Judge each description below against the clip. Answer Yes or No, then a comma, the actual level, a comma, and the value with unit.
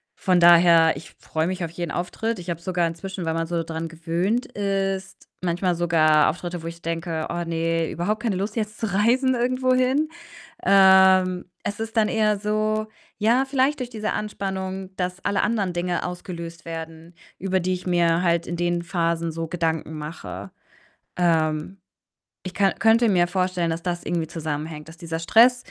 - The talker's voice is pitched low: No, medium, 180 Hz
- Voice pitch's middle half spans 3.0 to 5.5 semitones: Yes, average, 3.4 semitones